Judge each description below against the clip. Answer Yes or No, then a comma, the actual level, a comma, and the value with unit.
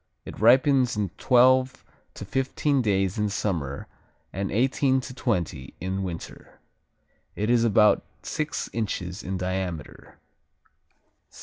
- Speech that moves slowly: Yes, slow, 115 wpm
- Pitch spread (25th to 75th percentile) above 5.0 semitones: Yes, wide, 5.4 semitones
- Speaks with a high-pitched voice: No, low, 105 Hz